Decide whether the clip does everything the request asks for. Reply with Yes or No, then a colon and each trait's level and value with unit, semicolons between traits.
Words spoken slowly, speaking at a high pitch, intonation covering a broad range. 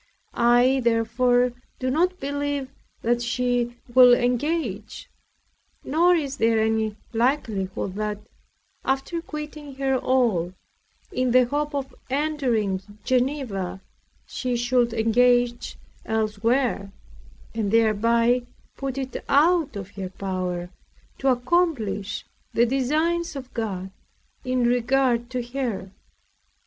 No: slow, 105 wpm; high, 245 Hz; average, 3.5 semitones